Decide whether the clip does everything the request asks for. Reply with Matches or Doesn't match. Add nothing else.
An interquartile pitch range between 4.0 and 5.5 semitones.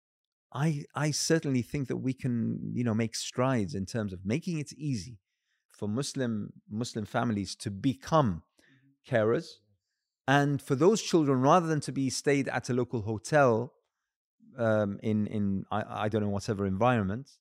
Matches